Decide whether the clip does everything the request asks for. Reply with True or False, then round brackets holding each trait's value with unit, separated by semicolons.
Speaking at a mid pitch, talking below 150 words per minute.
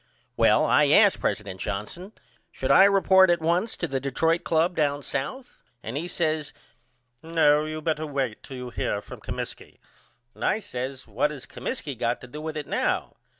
False (150 Hz; 180 wpm)